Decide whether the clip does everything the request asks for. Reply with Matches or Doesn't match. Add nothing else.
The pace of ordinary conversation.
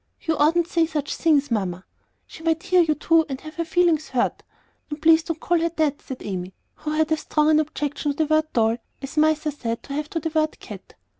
Doesn't match